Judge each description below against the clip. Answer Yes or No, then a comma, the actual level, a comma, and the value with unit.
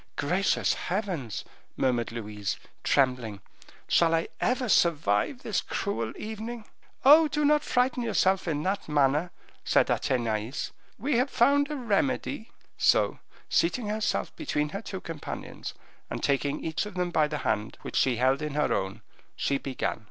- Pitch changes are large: Yes, wide, 8.7 semitones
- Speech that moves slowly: No, average, 150 wpm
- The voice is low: No, medium, 165 Hz